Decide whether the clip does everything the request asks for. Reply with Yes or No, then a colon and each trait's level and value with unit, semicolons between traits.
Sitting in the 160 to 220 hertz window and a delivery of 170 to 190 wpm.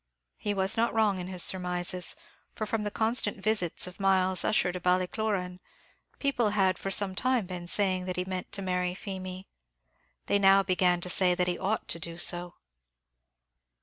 Yes: medium, 185 Hz; average, 180 wpm